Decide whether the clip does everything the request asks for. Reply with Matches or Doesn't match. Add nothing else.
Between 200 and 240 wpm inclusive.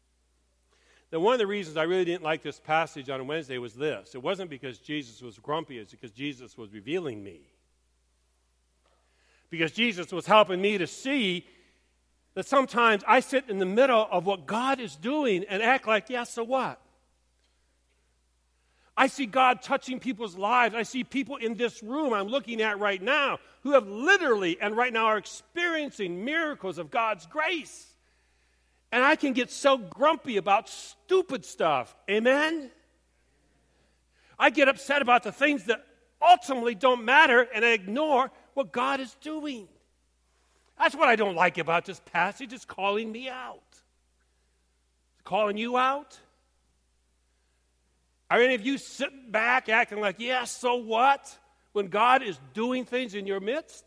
Doesn't match